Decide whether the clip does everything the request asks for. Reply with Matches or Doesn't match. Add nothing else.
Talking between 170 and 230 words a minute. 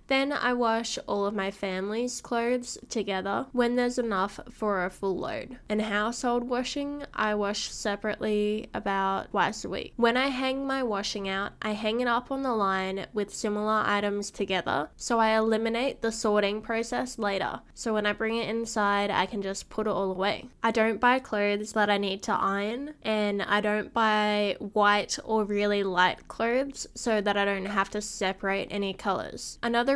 Matches